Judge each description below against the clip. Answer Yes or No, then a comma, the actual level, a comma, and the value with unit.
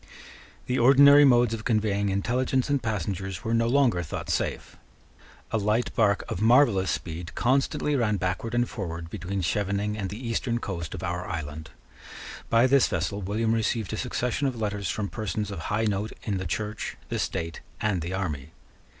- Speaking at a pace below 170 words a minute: No, average, 175 wpm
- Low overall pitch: Yes, low, 105 Hz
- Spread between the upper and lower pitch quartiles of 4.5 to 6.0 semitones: No, average, 4.0 semitones